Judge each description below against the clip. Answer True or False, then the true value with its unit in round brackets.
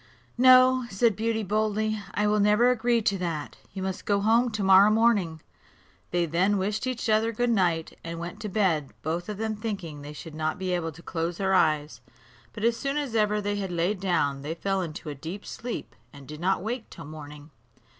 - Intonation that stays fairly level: False (4.7 semitones)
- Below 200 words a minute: False (205 wpm)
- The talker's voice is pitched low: False (195 Hz)